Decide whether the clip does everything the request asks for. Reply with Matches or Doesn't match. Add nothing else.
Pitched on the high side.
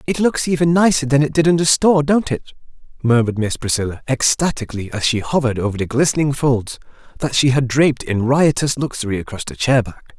Doesn't match